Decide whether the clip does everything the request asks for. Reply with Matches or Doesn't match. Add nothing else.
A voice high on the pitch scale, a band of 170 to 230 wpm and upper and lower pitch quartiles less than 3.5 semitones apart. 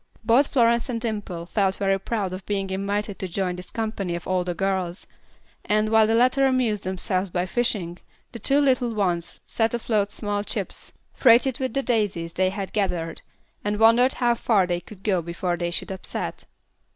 Doesn't match